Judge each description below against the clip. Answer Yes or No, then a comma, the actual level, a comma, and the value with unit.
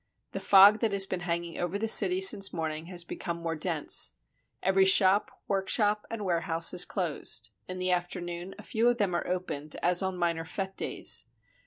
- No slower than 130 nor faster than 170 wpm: No, average, 185 wpm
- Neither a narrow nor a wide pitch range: No, narrow, 2.3 semitones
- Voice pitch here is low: No, medium, 180 Hz